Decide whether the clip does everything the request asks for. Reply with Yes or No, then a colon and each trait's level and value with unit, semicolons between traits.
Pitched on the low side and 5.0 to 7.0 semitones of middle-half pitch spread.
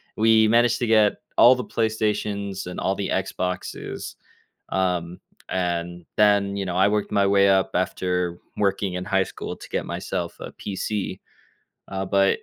No: low, 100 Hz; narrow, 2.4 semitones